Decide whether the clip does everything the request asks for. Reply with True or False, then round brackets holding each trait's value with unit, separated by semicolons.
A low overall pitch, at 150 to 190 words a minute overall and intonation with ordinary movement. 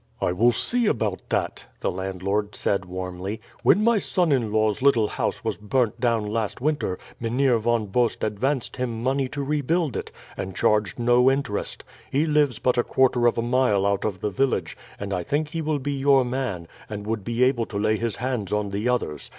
False (120 Hz; 200 wpm; 4.5 semitones)